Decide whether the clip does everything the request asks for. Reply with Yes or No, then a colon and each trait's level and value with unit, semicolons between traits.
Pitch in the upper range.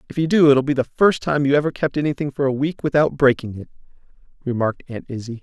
No: medium, 140 Hz